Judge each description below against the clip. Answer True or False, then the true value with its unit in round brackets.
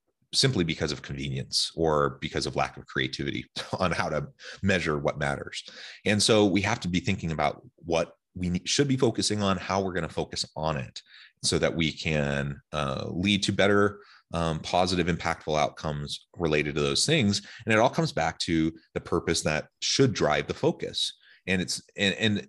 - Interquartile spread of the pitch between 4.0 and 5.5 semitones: True (4.9 semitones)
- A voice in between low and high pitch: False (90 Hz)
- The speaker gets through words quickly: False (185 wpm)